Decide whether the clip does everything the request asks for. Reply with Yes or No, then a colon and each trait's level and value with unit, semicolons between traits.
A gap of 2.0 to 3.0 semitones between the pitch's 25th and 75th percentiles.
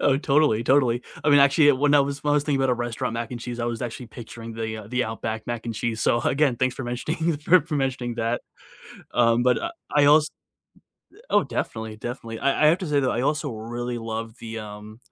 No: average, 3.8 semitones